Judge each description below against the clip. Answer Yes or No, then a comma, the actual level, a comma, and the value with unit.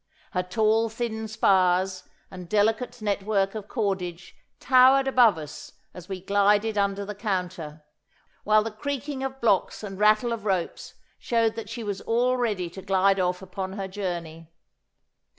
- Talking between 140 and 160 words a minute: Yes, average, 150 wpm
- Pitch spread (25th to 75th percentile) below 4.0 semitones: Yes, average, 3.1 semitones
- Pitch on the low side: No, high, 205 Hz